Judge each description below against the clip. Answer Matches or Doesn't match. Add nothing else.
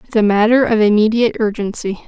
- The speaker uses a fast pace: Doesn't match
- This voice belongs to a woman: Matches